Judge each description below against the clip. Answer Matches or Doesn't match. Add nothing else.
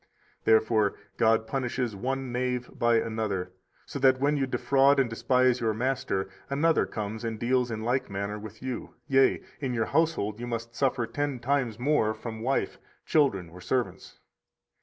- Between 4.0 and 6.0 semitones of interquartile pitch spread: Doesn't match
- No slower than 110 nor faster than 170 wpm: Matches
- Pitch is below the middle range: Matches